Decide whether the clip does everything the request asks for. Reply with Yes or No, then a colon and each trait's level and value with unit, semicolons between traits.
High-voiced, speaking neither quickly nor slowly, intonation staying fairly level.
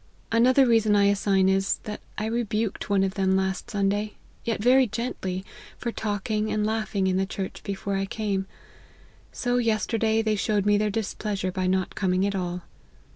Yes: high, 205 Hz; average, 170 wpm; narrow, 2.3 semitones